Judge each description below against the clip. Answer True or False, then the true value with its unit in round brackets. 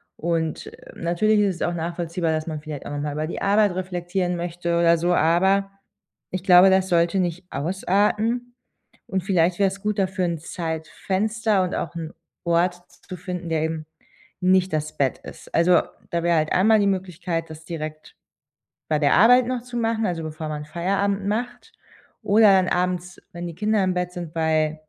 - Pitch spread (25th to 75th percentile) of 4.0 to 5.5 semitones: False (2.9 semitones)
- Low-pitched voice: False (175 Hz)